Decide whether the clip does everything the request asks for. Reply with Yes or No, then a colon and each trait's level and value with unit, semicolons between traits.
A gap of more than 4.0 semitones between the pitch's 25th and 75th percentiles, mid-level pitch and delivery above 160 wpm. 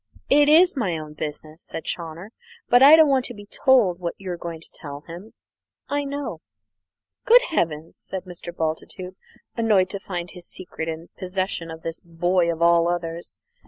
Yes: average, 5.0 semitones; medium, 175 Hz; average, 175 wpm